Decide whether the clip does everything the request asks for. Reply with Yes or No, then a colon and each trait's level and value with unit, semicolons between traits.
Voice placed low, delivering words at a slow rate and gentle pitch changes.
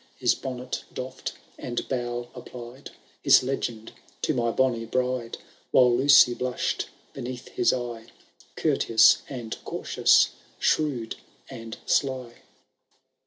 Yes: low, 125 Hz; slow, 110 wpm; narrow, 1.5 semitones